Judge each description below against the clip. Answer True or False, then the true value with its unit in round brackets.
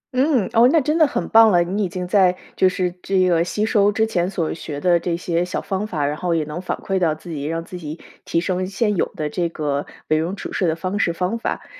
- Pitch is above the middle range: False (180 Hz)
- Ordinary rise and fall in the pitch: True (3.3 semitones)